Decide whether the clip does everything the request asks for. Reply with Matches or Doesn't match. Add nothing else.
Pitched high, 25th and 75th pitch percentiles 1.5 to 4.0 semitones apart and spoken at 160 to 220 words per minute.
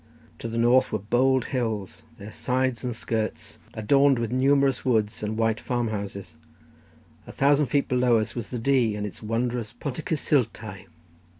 Doesn't match